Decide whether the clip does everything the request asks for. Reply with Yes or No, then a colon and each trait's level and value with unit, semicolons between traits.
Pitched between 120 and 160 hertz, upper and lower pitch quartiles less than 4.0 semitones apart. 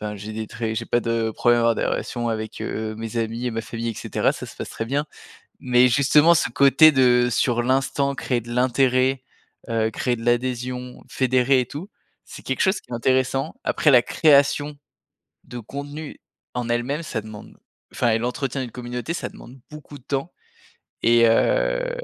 Yes: low, 125 Hz; average, 2.8 semitones